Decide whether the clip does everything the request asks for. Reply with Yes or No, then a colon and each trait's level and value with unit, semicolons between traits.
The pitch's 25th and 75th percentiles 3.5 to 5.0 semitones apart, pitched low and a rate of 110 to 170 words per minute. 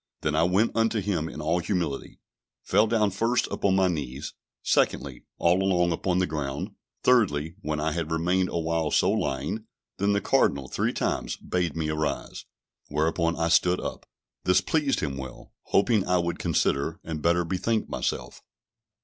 Yes: average, 3.8 semitones; very low, 85 Hz; average, 165 wpm